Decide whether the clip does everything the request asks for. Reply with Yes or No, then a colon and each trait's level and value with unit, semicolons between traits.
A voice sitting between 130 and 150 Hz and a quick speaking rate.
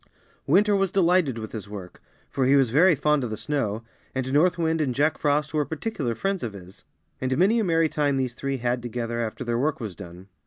Yes: low, 135 Hz; fast, 225 wpm